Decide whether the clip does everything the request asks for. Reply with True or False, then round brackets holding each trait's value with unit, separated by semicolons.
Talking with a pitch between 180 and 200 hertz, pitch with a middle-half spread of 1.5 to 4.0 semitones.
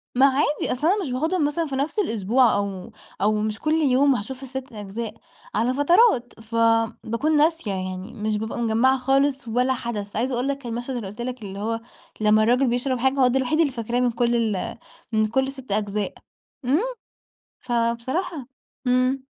False (245 Hz; 3.5 semitones)